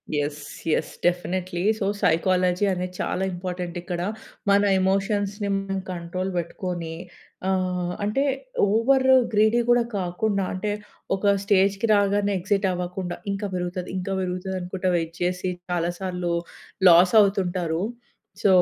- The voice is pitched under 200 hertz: Yes, medium, 185 Hz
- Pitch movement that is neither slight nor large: No, narrow, 2.1 semitones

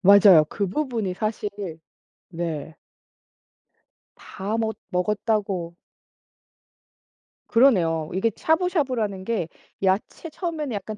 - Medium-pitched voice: No, high, 205 Hz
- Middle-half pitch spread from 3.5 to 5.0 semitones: Yes, average, 4.2 semitones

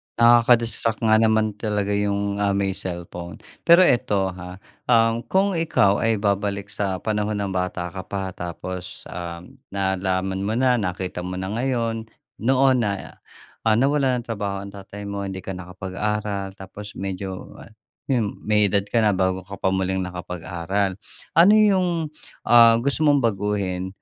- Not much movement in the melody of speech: No, average, 3.3 semitones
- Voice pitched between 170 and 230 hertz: No, low, 100 Hz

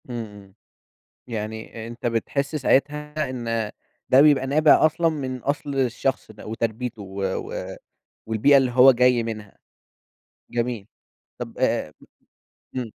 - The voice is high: No, low, 125 Hz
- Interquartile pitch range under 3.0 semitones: No, average, 3.8 semitones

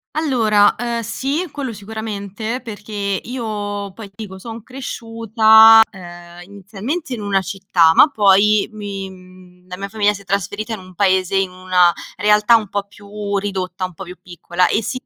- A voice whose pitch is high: Yes, high, 205 Hz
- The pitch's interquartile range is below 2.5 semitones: No, average, 2.8 semitones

